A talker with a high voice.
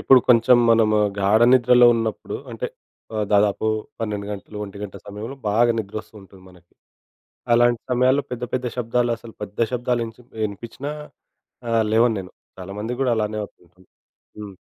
No: low, 110 Hz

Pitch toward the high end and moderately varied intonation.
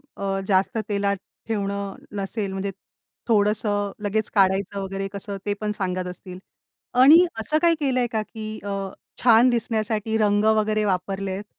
No: high, 205 Hz; narrow, 1.9 semitones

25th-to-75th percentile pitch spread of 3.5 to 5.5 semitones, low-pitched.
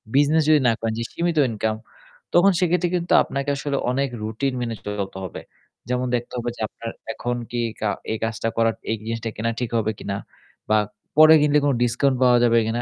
Yes: average, 4.2 semitones; low, 120 Hz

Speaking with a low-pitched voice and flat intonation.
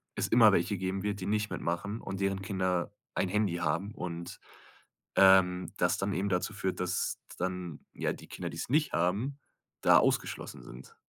Yes: very low, 95 Hz; narrow, 2.2 semitones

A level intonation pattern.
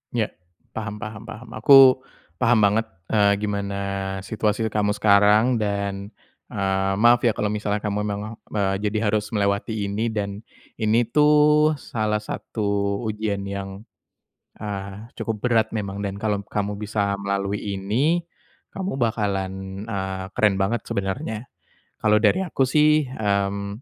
Yes: narrow, 1.9 semitones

